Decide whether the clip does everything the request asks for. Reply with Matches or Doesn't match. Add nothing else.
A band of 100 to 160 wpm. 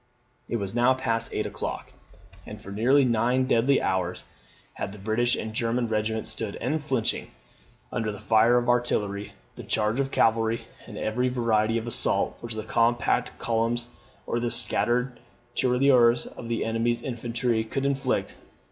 Matches